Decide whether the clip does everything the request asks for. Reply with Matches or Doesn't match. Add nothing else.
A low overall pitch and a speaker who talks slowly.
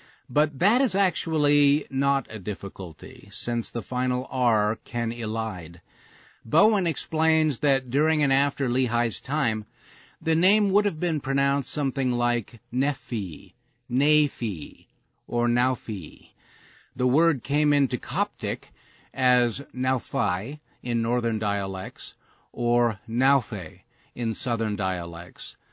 Matches